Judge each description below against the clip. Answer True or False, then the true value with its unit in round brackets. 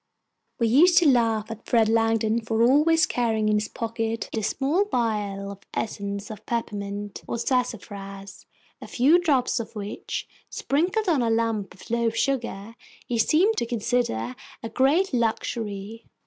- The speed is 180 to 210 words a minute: False (150 wpm)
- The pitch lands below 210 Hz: False (230 Hz)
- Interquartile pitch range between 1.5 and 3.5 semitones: True (3.2 semitones)